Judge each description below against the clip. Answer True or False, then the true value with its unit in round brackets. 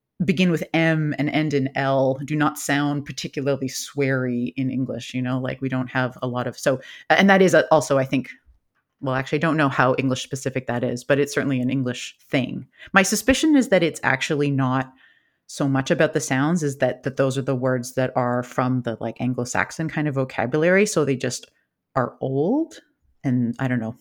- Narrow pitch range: False (3.0 semitones)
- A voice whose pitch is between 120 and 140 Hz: True (135 Hz)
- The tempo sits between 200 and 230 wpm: True (205 wpm)